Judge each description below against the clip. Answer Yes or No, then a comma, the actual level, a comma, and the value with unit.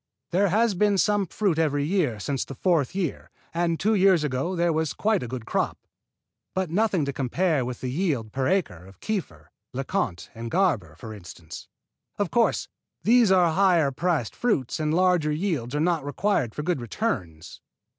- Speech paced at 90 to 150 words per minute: No, average, 175 wpm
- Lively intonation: Yes, wide, 6.7 semitones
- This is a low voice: No, medium, 160 Hz